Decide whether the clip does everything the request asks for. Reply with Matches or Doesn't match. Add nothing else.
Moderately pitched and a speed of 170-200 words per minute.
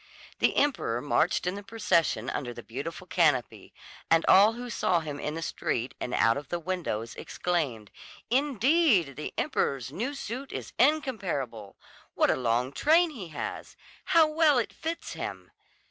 Doesn't match